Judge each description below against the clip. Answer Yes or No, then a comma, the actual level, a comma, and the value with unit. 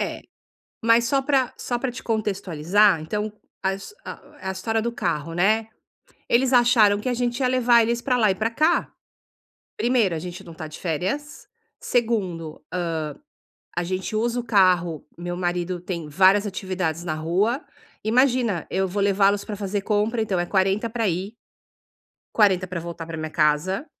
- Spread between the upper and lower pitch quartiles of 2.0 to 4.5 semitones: No, average, 4.9 semitones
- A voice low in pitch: No, high, 200 Hz